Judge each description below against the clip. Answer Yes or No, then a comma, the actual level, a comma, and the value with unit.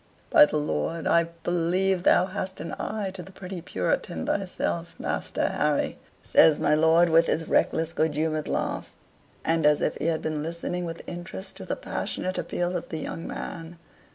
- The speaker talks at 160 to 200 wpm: Yes, average, 180 wpm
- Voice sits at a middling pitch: Yes, medium, 170 Hz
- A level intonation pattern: Yes, narrow, 2.3 semitones